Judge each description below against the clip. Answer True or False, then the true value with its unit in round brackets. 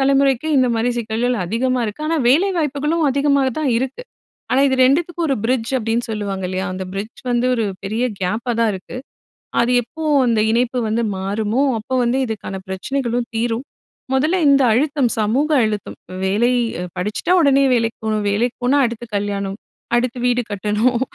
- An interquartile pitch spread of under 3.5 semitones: False (3.8 semitones)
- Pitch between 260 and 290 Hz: False (240 Hz)